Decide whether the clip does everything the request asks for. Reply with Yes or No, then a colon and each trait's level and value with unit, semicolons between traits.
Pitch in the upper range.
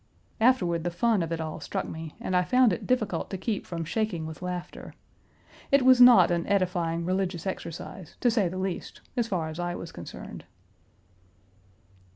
No: medium, 180 Hz